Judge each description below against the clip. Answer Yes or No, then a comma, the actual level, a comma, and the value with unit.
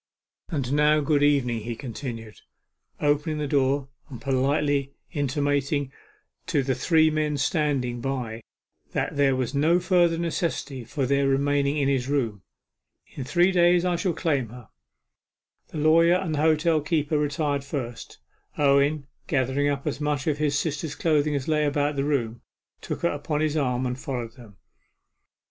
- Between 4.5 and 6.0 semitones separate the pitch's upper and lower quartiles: No, narrow, 2.5 semitones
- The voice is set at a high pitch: No, medium, 145 Hz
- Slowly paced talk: No, average, 160 wpm